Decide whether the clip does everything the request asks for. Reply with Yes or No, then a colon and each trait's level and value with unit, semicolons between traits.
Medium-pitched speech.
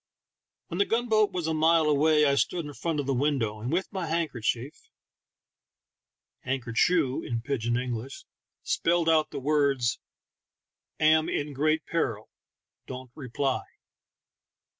Yes: medium, 145 Hz